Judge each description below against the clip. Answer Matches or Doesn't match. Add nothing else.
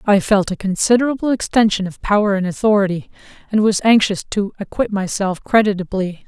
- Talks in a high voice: Matches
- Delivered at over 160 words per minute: Doesn't match